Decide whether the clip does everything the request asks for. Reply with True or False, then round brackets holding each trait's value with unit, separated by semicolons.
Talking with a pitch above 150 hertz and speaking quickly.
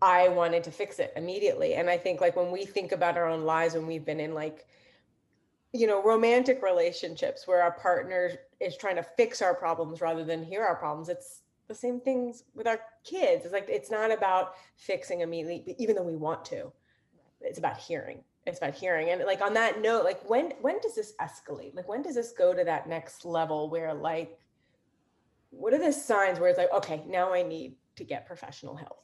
True (185 Hz; 210 wpm)